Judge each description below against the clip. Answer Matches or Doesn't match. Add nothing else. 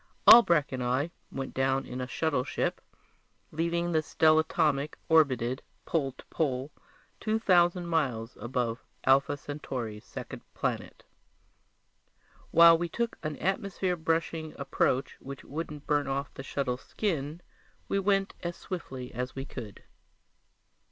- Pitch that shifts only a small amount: Doesn't match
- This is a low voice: Doesn't match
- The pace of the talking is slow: Matches